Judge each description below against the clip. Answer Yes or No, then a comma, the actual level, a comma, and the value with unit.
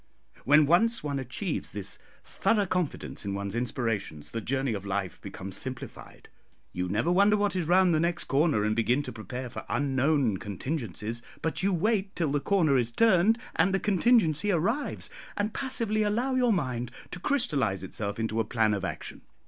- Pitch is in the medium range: Yes, medium, 145 Hz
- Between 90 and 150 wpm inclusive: No, average, 175 wpm